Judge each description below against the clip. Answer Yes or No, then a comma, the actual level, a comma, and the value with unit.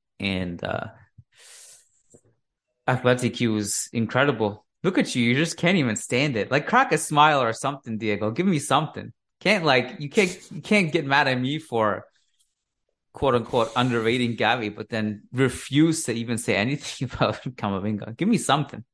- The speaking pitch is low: Yes, low, 125 Hz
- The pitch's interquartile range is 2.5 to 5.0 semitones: No, wide, 5.4 semitones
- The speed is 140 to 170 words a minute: Yes, average, 165 wpm